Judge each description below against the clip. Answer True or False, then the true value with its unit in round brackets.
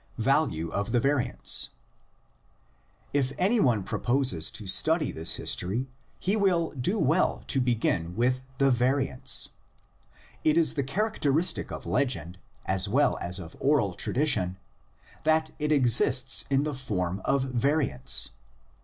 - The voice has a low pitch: True (130 Hz)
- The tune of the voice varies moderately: False (6.4 semitones)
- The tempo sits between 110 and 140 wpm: True (135 wpm)